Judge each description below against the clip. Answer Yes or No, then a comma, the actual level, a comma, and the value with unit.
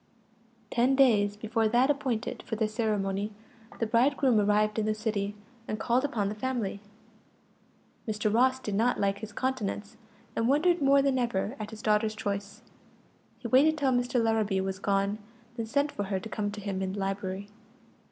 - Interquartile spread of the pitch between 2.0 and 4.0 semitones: Yes, average, 3.3 semitones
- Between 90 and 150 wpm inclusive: No, average, 175 wpm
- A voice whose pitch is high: Yes, high, 220 Hz